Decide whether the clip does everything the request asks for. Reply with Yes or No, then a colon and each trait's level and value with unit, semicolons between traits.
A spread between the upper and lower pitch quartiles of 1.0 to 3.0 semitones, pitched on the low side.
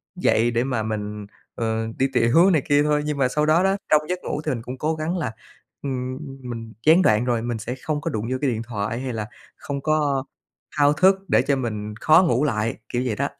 No: average, 5.0 semitones; low, 130 Hz